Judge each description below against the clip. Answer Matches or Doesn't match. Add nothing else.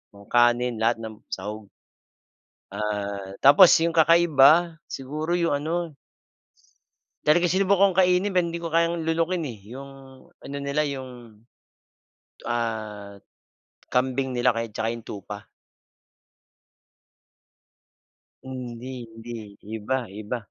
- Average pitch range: Doesn't match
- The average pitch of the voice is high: Doesn't match